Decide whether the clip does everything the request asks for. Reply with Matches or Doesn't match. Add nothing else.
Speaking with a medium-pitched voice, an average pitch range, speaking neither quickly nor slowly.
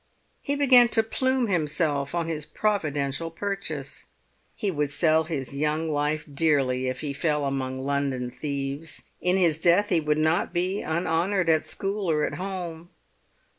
Matches